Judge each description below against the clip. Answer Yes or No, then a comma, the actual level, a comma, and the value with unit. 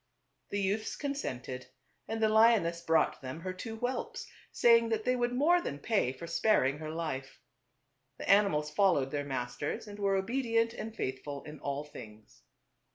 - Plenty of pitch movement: Yes, wide, 7.9 semitones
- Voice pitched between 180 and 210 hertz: Yes, high, 190 Hz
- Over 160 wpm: Yes, average, 190 wpm